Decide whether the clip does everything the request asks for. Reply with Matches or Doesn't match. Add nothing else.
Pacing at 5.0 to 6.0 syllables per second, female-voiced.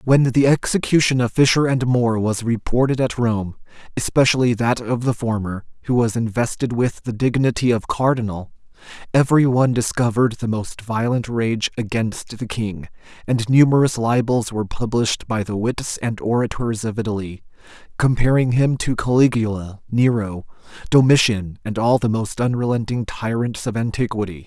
Doesn't match